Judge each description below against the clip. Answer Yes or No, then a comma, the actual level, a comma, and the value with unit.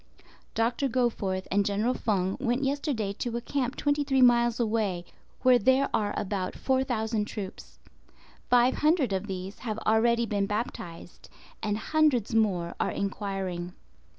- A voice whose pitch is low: No, high, 225 Hz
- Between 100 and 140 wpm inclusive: Yes, slow, 135 wpm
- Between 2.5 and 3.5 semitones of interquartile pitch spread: No, average, 4.1 semitones